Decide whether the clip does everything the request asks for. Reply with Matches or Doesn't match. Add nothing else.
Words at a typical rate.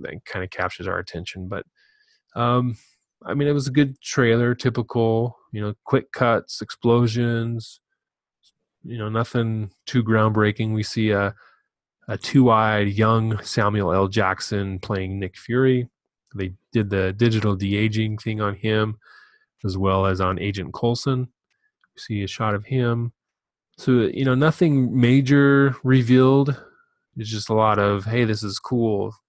Matches